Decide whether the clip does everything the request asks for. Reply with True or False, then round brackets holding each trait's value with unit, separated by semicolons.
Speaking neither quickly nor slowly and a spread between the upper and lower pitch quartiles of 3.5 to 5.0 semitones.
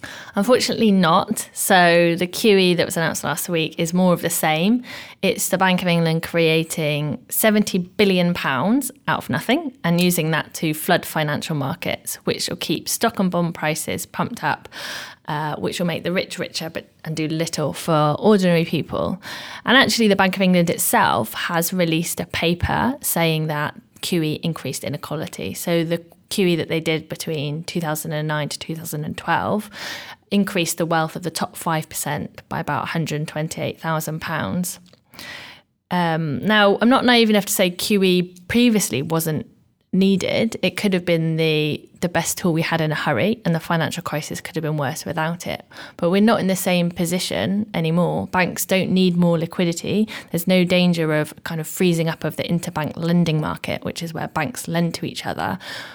False (175 wpm; 3.0 semitones)